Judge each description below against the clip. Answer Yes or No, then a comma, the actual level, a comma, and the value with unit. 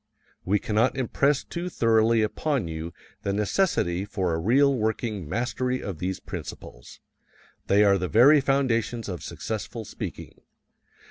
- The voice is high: No, low, 110 Hz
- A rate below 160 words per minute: Yes, slow, 135 wpm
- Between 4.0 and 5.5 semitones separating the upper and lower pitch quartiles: Yes, average, 4.7 semitones